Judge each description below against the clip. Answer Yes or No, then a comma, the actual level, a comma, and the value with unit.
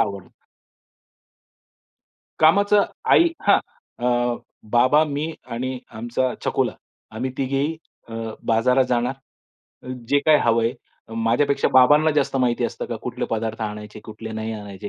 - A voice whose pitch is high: No, low, 125 Hz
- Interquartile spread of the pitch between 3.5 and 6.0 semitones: Yes, average, 4.0 semitones